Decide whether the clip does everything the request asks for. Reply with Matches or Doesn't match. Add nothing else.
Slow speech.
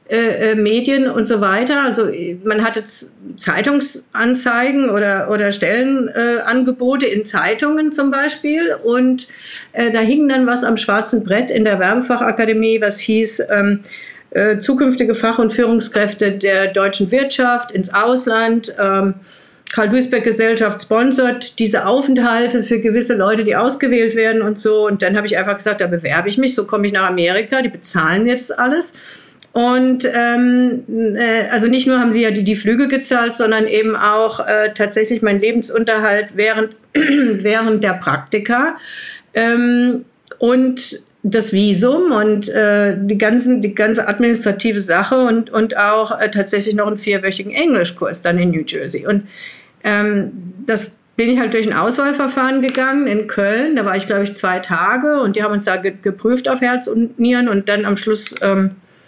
Doesn't match